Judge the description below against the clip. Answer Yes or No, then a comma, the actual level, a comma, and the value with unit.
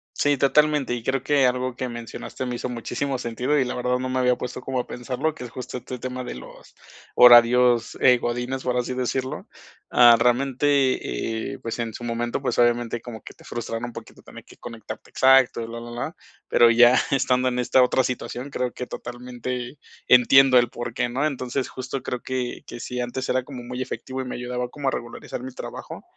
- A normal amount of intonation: No, narrow, 1.3 semitones